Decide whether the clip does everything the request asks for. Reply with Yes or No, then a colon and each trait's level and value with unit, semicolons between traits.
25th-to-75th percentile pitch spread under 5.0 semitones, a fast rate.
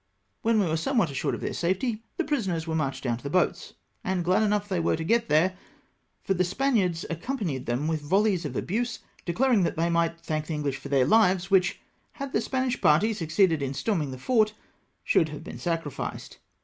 No: wide, 5.5 semitones; fast, 210 wpm